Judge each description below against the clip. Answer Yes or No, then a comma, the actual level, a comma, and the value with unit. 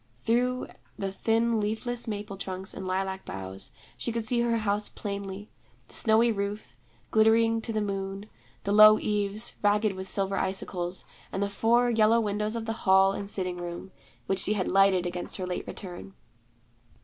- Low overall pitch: No, high, 205 Hz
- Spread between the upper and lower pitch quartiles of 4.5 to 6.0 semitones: No, narrow, 2.5 semitones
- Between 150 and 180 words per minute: Yes, average, 170 wpm